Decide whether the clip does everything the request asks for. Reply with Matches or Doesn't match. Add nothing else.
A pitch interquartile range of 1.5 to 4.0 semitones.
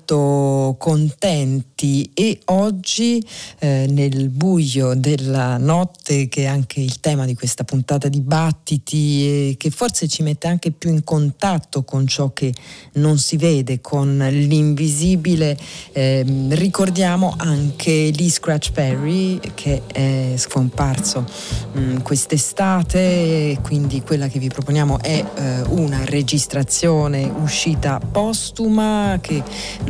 Matches